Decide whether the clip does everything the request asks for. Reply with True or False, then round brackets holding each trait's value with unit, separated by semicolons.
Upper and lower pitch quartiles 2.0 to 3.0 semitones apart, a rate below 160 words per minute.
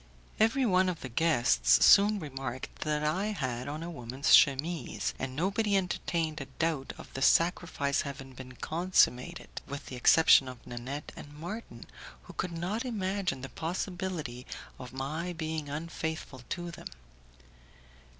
False (5.1 semitones; 145 wpm)